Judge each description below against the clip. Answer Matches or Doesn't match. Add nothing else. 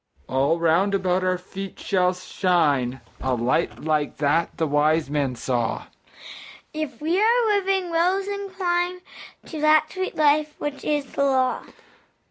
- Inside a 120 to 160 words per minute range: Matches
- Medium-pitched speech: Doesn't match